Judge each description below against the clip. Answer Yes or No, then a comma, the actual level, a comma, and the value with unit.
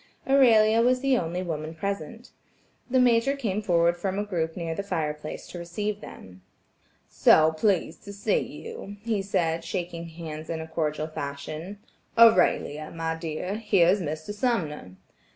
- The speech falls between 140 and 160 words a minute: Yes, average, 155 wpm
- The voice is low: No, medium, 175 Hz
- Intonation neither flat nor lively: Yes, average, 4.7 semitones